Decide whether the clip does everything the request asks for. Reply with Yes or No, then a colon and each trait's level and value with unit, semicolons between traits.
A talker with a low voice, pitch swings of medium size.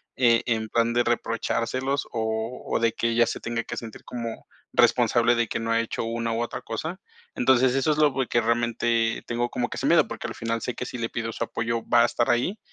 No: low, 115 Hz; narrow, 1.0 semitones